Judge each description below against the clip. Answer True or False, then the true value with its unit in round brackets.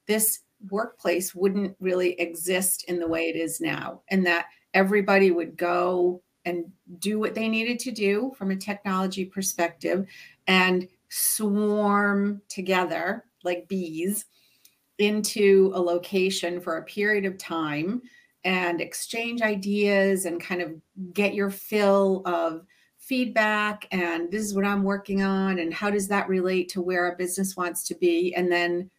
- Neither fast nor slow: True (150 wpm)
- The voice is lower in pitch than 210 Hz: True (190 Hz)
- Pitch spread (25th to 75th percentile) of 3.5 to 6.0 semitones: False (2.5 semitones)